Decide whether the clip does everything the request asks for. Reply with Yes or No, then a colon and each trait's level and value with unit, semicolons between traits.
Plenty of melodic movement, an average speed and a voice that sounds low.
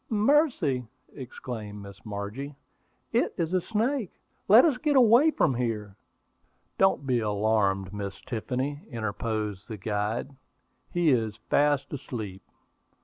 No: wide, 8.5 semitones; slow, 120 wpm; low, 120 Hz